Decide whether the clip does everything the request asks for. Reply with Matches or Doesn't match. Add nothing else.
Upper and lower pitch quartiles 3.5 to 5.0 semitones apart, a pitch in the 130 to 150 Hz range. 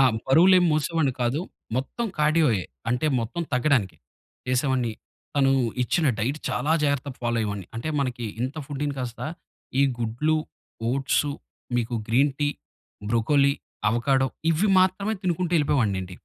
Matches